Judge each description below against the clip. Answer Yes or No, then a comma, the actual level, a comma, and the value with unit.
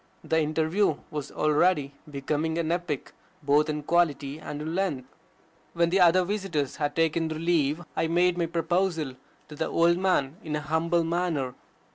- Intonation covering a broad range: No, narrow, 2.5 semitones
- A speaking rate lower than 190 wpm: Yes, average, 165 wpm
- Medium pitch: Yes, medium, 160 Hz